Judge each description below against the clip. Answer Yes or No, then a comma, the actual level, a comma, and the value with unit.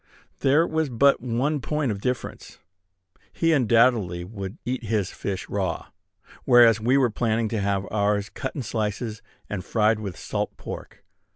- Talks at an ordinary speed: Yes, average, 155 wpm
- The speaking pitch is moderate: No, low, 115 Hz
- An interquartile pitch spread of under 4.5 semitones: Yes, average, 3.9 semitones